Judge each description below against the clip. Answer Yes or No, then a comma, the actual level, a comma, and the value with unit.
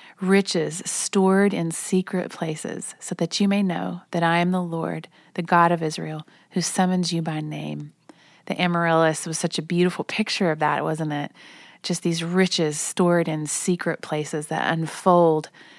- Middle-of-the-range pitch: Yes, medium, 170 Hz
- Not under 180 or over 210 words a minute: No, average, 165 wpm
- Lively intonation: No, narrow, 2.4 semitones